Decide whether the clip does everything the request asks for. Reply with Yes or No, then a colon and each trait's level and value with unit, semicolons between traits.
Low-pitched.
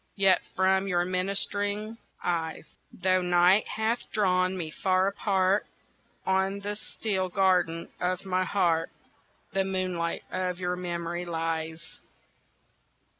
No: medium, 185 Hz